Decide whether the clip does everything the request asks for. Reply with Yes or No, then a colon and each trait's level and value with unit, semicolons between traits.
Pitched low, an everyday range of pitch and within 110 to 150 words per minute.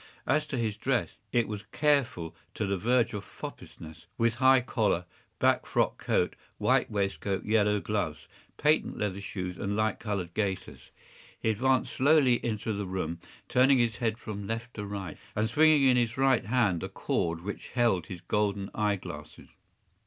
No: low, 105 Hz; average, 3.8 semitones; average, 165 wpm